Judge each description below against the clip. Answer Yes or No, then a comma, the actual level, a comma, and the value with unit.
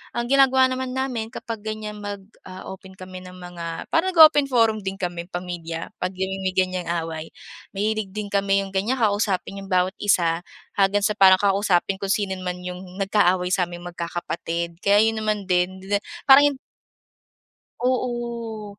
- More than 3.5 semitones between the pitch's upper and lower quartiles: No, average, 3.1 semitones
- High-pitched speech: Yes, high, 195 Hz